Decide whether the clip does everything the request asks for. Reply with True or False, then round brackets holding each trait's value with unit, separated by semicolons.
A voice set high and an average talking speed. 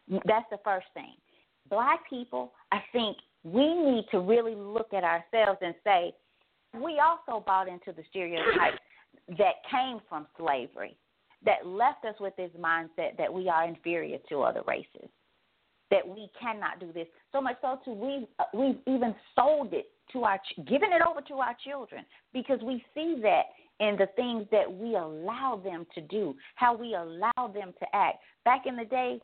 True (225 Hz; 175 wpm)